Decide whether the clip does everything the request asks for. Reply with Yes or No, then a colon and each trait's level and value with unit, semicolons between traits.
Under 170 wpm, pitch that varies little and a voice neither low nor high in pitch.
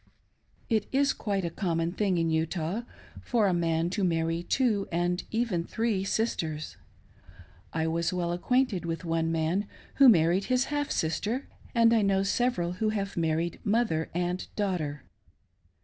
No: average, 150 wpm; average, 4.9 semitones; medium, 180 Hz